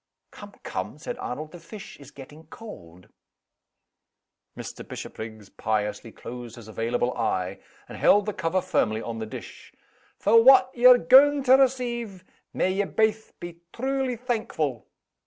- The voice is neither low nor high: Yes, medium, 180 Hz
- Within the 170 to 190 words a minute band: No, average, 140 wpm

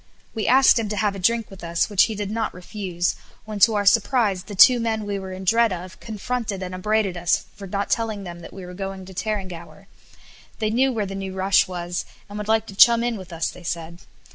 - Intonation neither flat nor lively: Yes, average, 3.1 semitones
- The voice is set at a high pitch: Yes, high, 200 Hz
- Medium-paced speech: No, fast, 240 wpm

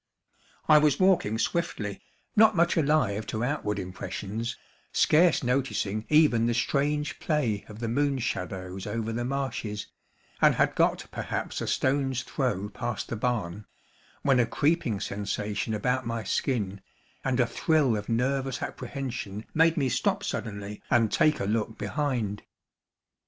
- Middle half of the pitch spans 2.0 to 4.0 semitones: No, average, 5.2 semitones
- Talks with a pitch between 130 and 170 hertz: No, low, 120 Hz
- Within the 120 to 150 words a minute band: Yes, average, 140 wpm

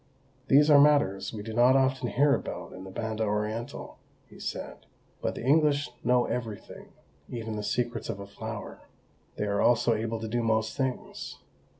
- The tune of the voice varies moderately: Yes, average, 3.4 semitones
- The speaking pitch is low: Yes, low, 115 Hz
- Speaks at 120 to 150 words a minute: No, average, 175 wpm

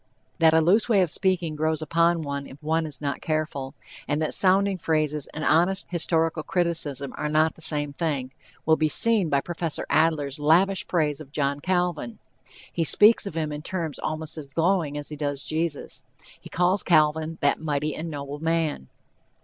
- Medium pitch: Yes, medium, 155 Hz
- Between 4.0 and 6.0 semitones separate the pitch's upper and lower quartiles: No, narrow, 2.5 semitones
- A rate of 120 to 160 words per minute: No, average, 185 wpm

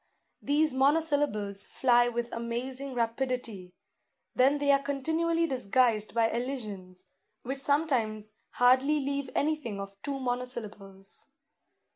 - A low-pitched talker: No, very high, 250 Hz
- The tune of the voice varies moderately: Yes, average, 4.4 semitones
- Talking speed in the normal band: No, slow, 105 wpm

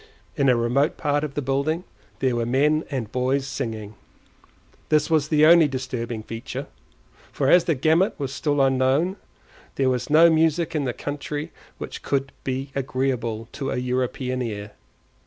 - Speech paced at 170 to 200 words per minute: No, average, 160 wpm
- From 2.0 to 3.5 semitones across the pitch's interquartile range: Yes, average, 3.0 semitones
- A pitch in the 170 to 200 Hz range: No, low, 135 Hz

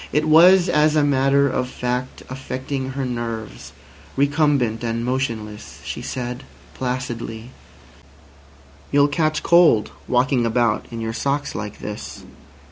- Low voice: Yes, low, 130 Hz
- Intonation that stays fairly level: No, average, 3.6 semitones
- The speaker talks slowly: Yes, slow, 125 wpm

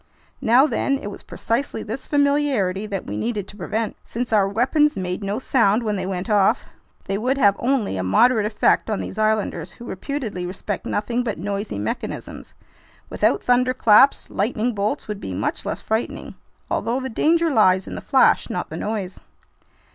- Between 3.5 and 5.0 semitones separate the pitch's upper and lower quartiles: Yes, average, 4.1 semitones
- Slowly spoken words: No, average, 175 wpm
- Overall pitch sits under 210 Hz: No, high, 215 Hz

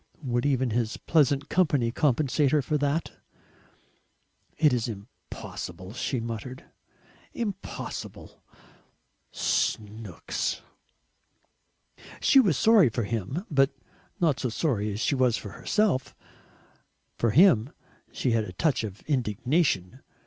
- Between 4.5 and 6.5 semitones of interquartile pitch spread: Yes, average, 5.2 semitones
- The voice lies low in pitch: Yes, low, 130 Hz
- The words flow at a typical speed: No, slow, 115 wpm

